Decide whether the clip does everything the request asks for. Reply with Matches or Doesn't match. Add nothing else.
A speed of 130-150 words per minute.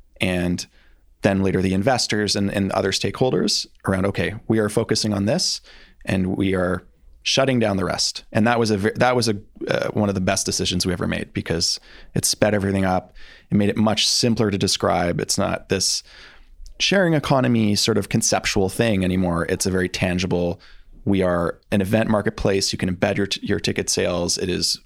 Doesn't match